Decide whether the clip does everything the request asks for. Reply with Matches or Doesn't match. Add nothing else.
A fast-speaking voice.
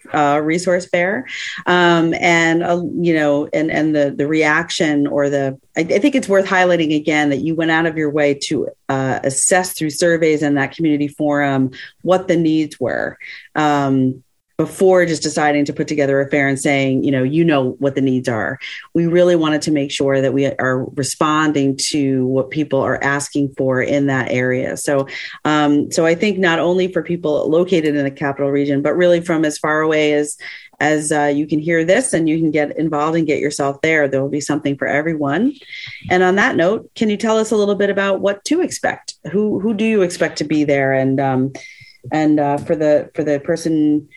Matches